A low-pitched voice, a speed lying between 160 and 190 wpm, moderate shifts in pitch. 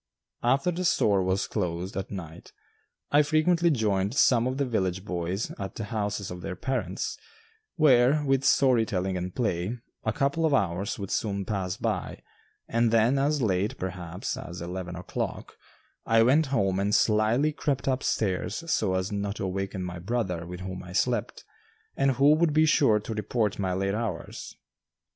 No: low, 105 Hz; average, 170 wpm; wide, 5.9 semitones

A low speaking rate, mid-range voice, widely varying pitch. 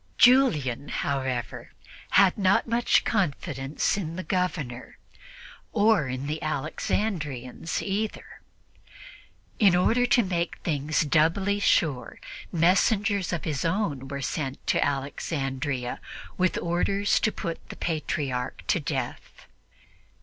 Yes: slow, 110 wpm; medium, 165 Hz; wide, 6.1 semitones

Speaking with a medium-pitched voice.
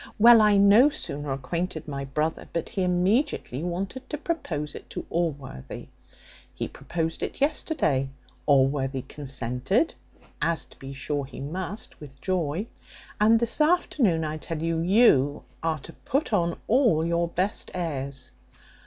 Yes: medium, 165 Hz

